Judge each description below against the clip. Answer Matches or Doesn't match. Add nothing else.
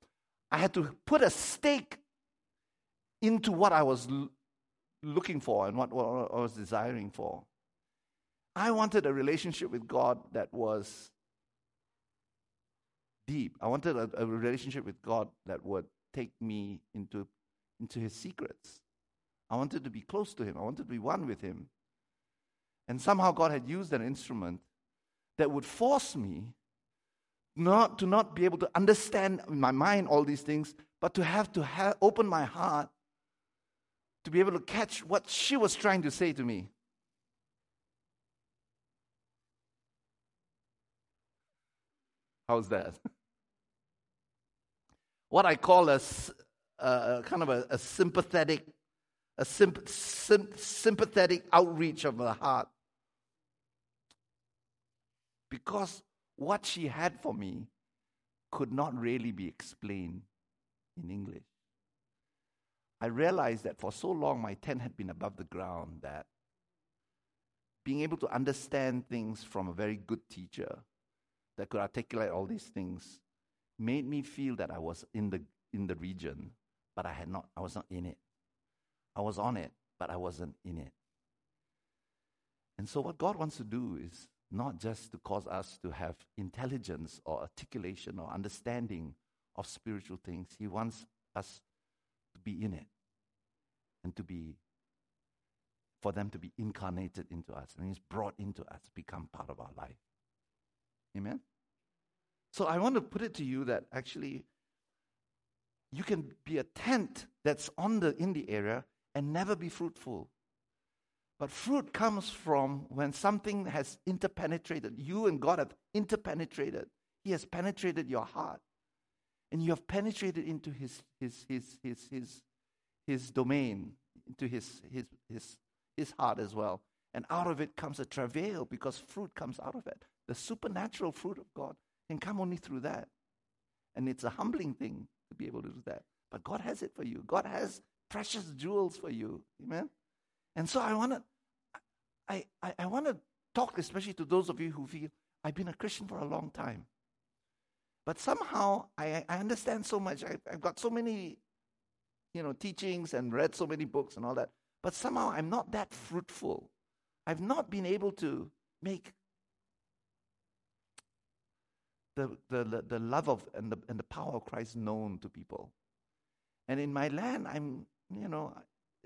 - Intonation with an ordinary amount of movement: Doesn't match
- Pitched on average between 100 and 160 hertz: Matches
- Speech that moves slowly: Doesn't match